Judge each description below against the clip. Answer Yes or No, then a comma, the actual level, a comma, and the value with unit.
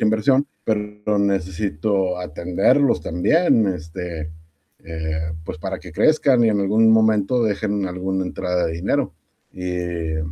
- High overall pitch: No, very low, 95 Hz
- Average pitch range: Yes, average, 3.7 semitones